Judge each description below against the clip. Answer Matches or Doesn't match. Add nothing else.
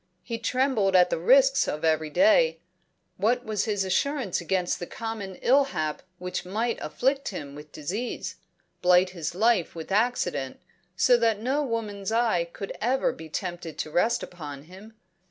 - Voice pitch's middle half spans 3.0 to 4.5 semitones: Doesn't match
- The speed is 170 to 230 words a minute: Doesn't match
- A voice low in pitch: Doesn't match